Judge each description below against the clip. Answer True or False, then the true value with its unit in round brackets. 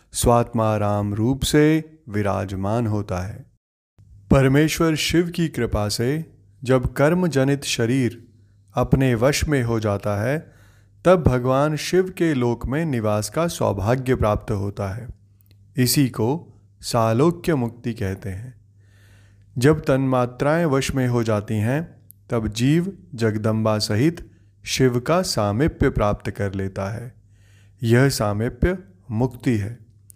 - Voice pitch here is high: False (120 Hz)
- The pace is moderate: True (120 wpm)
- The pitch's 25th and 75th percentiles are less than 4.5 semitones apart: False (5.0 semitones)